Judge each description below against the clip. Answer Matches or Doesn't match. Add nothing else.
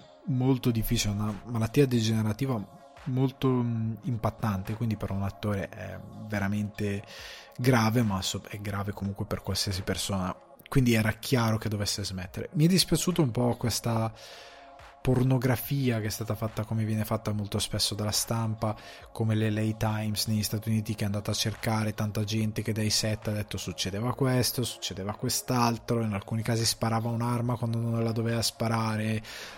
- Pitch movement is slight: Matches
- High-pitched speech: Doesn't match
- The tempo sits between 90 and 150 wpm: Doesn't match